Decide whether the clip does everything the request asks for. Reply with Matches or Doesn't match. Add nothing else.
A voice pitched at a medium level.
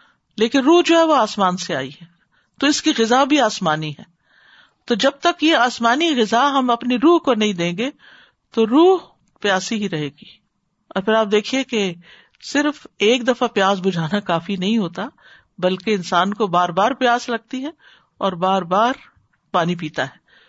Doesn't match